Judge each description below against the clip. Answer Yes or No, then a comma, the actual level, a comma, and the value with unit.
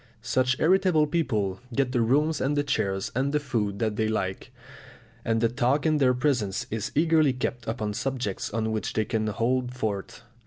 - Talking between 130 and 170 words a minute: No, average, 185 wpm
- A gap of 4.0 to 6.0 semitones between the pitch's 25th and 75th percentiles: Yes, average, 4.5 semitones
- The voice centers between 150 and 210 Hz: No, low, 125 Hz